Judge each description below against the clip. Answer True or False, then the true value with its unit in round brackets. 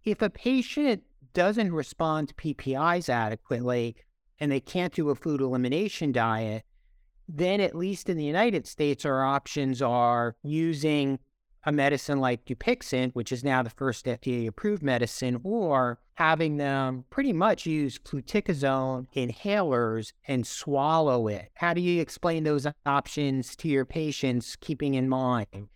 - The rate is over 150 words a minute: False (145 wpm)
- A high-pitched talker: False (140 Hz)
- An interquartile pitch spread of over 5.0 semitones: False (4.5 semitones)